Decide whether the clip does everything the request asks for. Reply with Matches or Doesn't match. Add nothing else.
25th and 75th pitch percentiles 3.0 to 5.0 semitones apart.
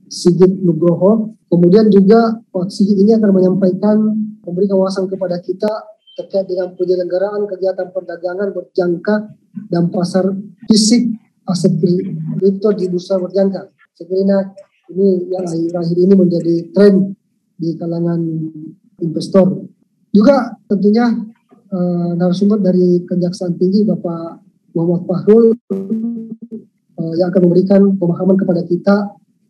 Doesn't match